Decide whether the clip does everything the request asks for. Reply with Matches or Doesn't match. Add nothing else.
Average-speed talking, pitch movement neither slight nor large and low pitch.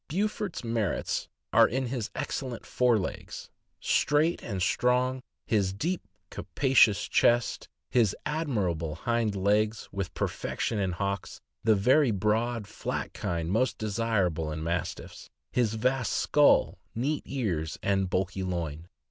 Doesn't match